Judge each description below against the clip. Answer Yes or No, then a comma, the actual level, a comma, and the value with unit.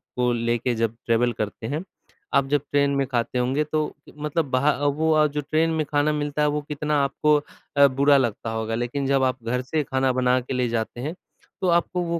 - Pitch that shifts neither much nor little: Yes, average, 3.3 semitones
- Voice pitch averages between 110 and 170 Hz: Yes, medium, 140 Hz